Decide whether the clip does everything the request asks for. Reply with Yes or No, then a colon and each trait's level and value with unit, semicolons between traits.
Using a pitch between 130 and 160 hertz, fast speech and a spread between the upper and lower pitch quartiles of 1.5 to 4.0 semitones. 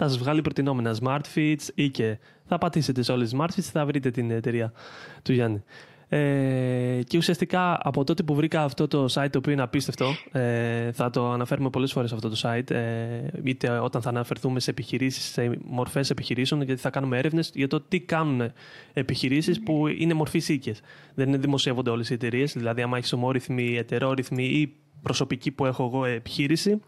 Yes: low, 135 Hz; fast, 185 wpm; average, 3.3 semitones